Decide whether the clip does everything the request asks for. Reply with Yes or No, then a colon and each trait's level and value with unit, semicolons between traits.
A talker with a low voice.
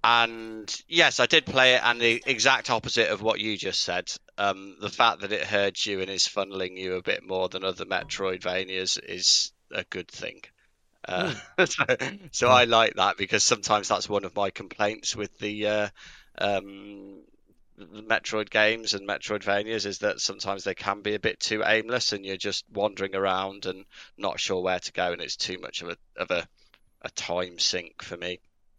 Yes: low, 100 Hz